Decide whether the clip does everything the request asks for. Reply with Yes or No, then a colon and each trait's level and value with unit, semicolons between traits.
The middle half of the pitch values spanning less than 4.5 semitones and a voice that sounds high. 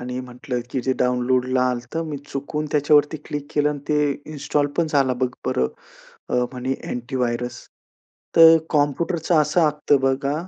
No: average, 2.9 semitones; medium, 140 Hz